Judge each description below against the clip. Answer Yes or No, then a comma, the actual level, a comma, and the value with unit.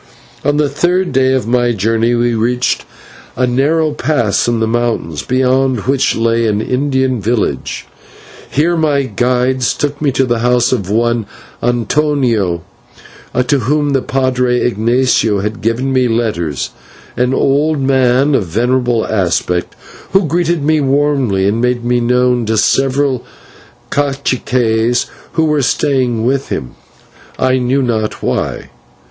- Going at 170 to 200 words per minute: No, average, 140 wpm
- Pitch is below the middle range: Yes, low, 125 Hz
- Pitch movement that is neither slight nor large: Yes, average, 3.0 semitones